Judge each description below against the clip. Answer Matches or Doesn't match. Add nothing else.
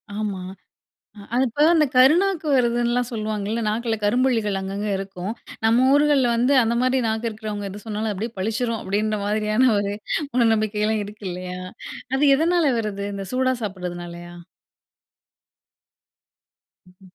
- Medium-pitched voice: Doesn't match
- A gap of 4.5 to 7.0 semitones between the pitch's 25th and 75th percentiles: Doesn't match